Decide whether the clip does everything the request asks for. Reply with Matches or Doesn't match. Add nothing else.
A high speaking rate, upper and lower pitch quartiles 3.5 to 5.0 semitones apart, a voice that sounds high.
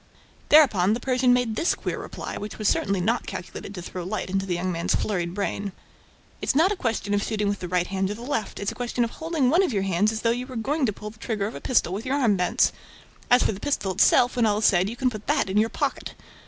Matches